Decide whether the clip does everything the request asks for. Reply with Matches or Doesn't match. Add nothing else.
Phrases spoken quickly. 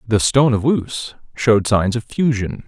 Doesn't match